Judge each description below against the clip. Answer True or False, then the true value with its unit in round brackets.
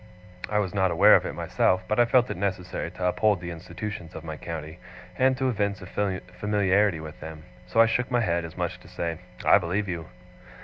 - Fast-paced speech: True (220 wpm)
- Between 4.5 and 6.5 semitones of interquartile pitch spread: False (3.8 semitones)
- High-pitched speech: False (95 Hz)